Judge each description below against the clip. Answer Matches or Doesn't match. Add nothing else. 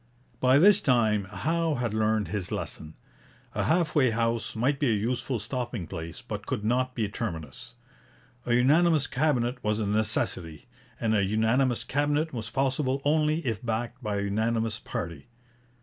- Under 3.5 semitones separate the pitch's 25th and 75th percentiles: Doesn't match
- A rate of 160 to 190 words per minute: Matches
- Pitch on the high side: Doesn't match